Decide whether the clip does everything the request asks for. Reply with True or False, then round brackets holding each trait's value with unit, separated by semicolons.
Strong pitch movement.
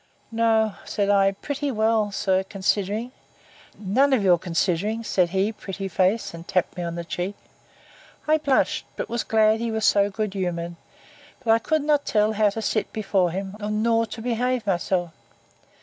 False (3.1 semitones)